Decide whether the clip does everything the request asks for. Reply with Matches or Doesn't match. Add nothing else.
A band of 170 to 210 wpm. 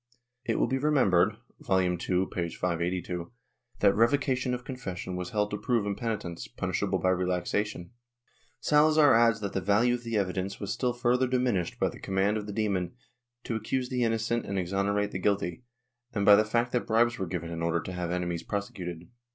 Matches